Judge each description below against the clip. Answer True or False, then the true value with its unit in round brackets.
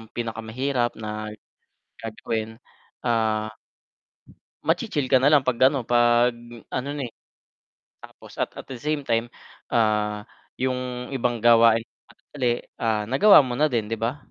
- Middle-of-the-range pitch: False (120 Hz)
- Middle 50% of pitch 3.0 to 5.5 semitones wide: False (2.4 semitones)